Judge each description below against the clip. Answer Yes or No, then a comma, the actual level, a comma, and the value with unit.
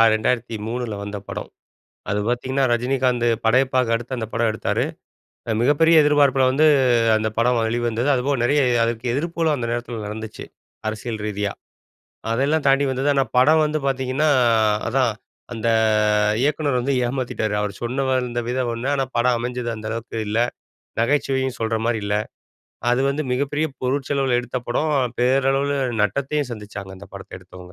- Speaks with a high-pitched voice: No, low, 125 Hz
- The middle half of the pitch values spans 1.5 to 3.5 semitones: Yes, average, 3.2 semitones